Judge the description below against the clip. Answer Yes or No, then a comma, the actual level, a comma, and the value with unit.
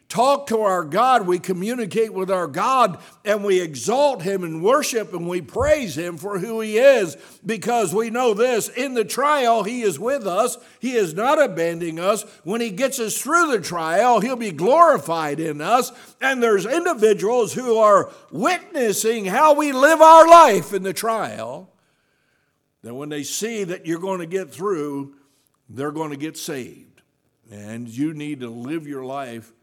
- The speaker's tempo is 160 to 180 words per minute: Yes, average, 175 wpm